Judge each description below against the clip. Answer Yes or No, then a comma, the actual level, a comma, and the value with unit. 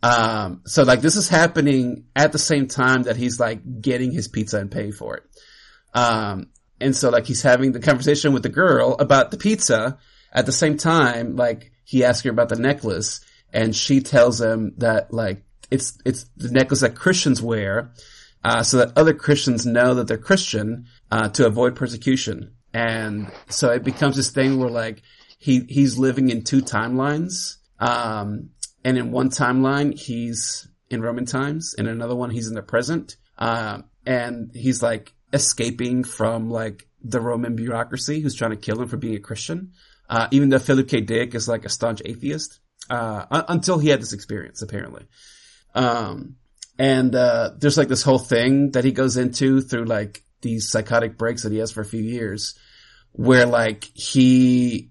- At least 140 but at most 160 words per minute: No, average, 180 wpm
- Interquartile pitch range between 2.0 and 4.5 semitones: Yes, average, 2.9 semitones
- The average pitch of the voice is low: Yes, low, 125 Hz